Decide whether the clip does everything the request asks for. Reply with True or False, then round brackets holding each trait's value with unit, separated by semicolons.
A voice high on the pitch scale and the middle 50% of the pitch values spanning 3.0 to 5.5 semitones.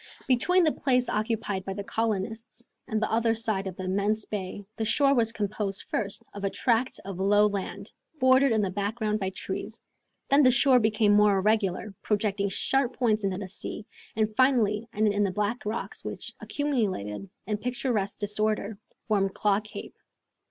False (215 Hz; 2.6 semitones)